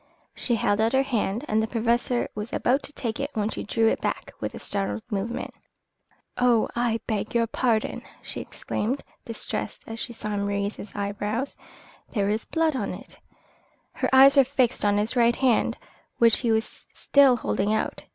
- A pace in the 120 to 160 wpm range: No, average, 185 wpm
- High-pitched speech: Yes, high, 230 Hz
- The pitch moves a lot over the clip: No, average, 2.8 semitones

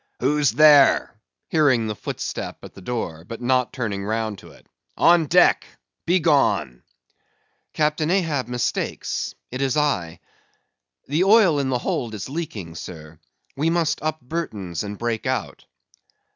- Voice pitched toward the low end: Yes, low, 130 Hz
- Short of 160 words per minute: Yes, average, 140 wpm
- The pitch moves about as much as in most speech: No, wide, 6.3 semitones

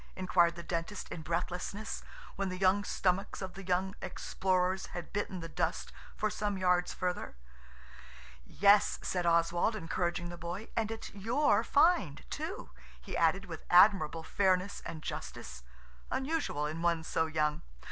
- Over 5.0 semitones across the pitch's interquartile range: No, average, 3.0 semitones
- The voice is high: No, medium, 180 Hz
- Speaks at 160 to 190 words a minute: No, average, 145 wpm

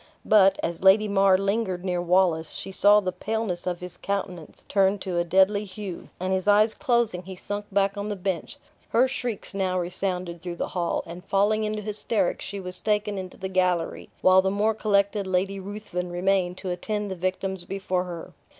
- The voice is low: No, high, 190 Hz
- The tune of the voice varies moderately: No, narrow, 2.2 semitones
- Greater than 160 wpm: Yes, average, 190 wpm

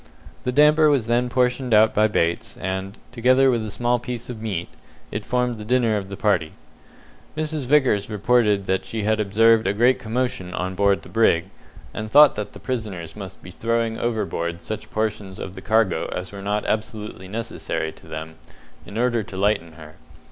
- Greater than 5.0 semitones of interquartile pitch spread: No, average, 3.9 semitones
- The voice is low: Yes, low, 110 Hz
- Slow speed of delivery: No, average, 185 wpm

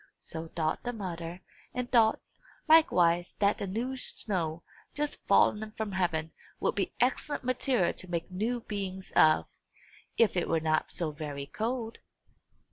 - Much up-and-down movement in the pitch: Yes, wide, 5.7 semitones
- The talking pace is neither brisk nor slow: Yes, average, 145 wpm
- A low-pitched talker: No, high, 190 Hz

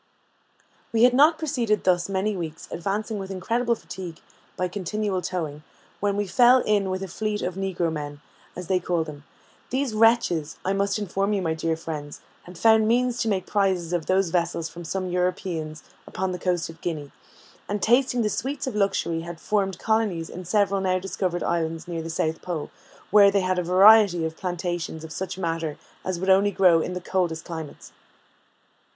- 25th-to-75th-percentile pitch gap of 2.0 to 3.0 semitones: No, average, 3.6 semitones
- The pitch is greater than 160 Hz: Yes, medium, 185 Hz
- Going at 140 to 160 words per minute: No, average, 185 wpm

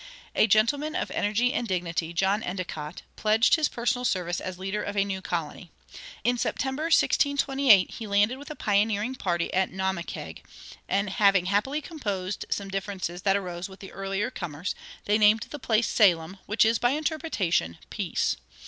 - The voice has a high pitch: Yes, high, 200 Hz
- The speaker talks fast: No, average, 165 wpm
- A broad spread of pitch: No, average, 4.3 semitones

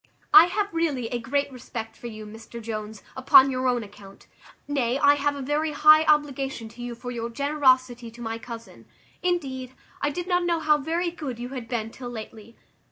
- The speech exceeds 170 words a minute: Yes, average, 195 wpm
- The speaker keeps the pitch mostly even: No, average, 4.2 semitones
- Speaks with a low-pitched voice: No, very high, 260 Hz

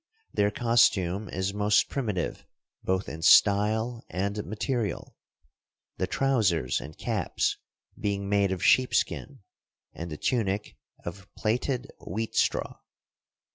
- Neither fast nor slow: No, slow, 110 wpm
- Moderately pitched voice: No, low, 105 Hz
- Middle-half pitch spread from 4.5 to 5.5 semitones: No, average, 3.4 semitones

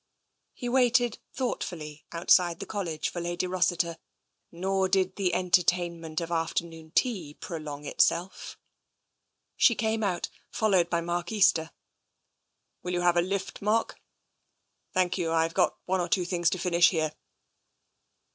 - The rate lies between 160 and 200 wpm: No, average, 145 wpm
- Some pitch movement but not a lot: No, narrow, 2.2 semitones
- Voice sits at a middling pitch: Yes, medium, 175 Hz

